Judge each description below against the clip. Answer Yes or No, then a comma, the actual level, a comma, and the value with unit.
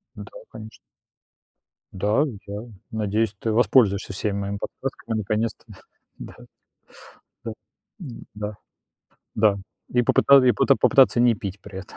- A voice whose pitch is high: No, low, 110 Hz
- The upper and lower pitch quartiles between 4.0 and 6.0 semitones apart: No, average, 2.8 semitones